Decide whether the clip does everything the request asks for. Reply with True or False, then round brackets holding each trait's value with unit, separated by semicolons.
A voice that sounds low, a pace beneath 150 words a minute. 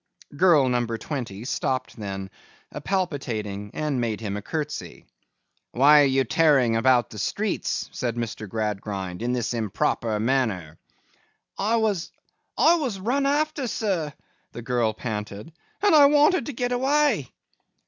True (130 Hz; 135 wpm)